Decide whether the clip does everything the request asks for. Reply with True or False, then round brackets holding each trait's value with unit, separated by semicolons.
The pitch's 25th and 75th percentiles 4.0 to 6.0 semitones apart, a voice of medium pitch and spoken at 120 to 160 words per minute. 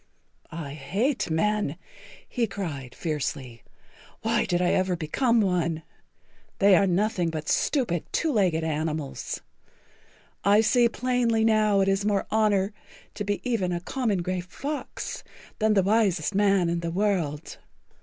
False (4.5 semitones; 195 Hz; 145 wpm)